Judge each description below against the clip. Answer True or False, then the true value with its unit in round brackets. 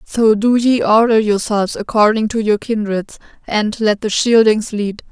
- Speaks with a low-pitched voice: False (215 Hz)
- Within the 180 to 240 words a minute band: False (165 wpm)